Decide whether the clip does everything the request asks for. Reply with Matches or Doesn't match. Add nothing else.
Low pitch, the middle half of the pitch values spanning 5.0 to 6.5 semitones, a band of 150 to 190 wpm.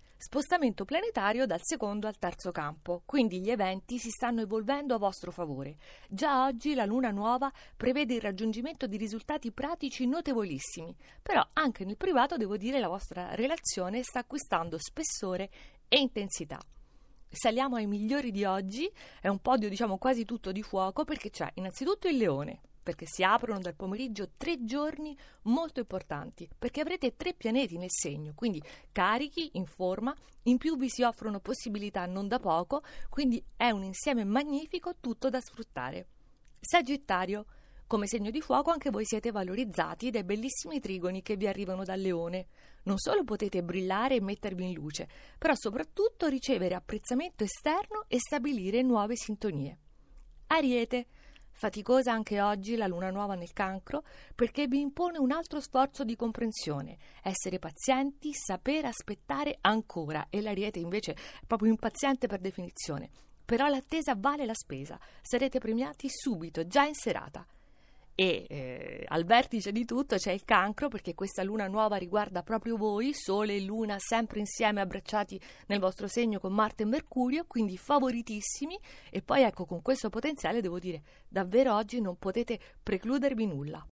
Doesn't match